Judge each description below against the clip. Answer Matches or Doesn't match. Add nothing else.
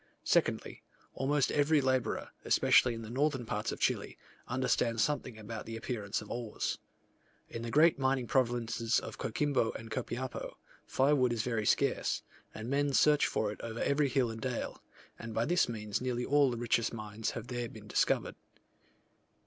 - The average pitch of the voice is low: Matches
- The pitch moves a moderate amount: Matches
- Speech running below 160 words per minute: Doesn't match